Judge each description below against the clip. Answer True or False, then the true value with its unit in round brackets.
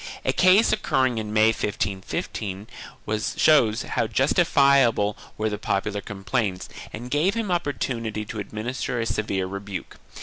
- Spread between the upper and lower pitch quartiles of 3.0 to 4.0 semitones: False (4.4 semitones)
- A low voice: True (110 Hz)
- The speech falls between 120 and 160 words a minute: True (140 wpm)